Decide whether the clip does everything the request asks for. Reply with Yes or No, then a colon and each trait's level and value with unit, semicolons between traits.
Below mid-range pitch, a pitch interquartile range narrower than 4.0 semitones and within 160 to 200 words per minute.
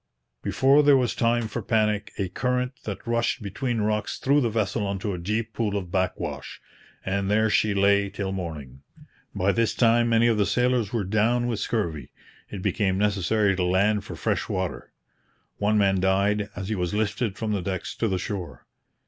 Yes: low, 105 Hz; average, 3.1 semitones; average, 185 wpm